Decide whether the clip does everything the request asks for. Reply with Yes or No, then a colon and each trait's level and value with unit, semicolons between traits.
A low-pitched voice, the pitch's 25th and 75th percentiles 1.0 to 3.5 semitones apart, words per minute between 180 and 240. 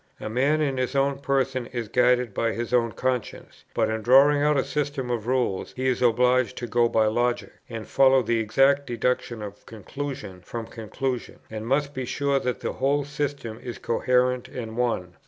Yes: low, 125 Hz; average, 2.8 semitones; average, 190 wpm